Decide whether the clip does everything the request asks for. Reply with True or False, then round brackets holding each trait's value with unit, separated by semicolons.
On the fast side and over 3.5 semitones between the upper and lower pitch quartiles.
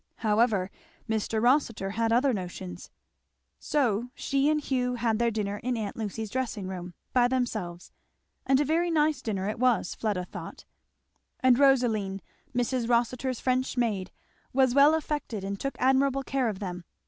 False (155 wpm; 4.1 semitones)